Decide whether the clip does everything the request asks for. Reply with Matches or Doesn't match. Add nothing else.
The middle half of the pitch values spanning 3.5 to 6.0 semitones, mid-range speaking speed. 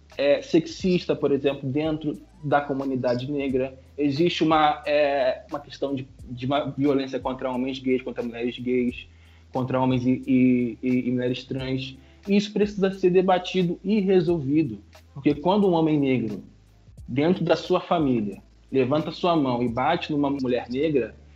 Matches